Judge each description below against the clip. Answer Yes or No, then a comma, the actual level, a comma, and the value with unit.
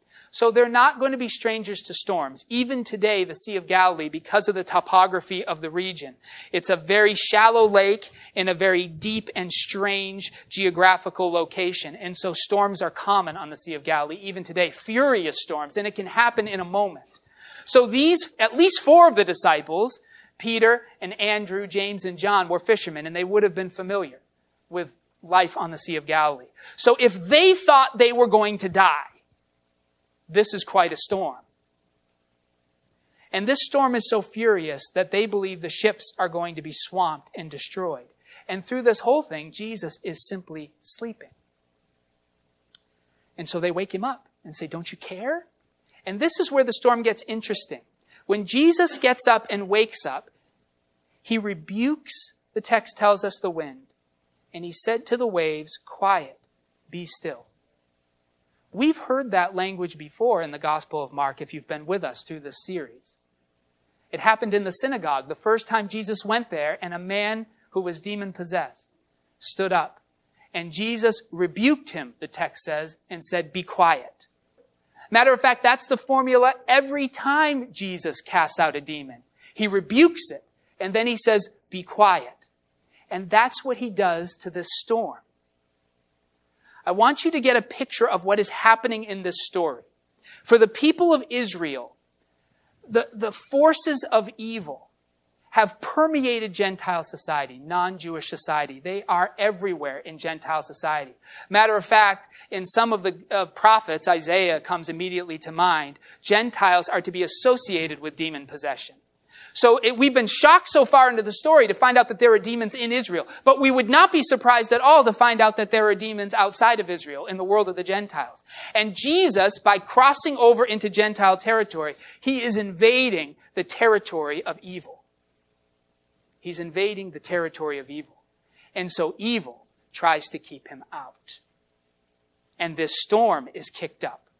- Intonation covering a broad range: Yes, wide, 6.3 semitones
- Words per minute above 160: Yes, average, 170 wpm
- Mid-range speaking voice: No, high, 195 Hz